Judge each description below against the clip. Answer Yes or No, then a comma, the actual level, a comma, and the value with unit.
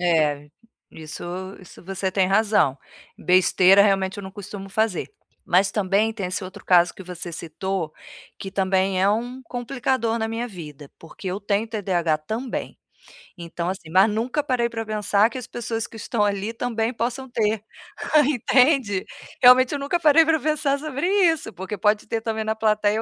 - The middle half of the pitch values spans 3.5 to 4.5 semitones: Yes, average, 4.0 semitones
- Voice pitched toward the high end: Yes, high, 210 Hz